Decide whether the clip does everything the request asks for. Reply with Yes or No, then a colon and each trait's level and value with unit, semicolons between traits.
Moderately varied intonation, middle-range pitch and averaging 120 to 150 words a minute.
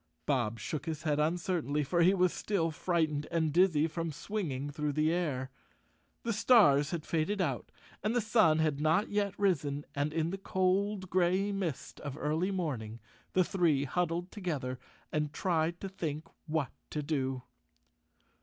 No: average, 4.0 semitones; medium, 160 Hz; average, 160 wpm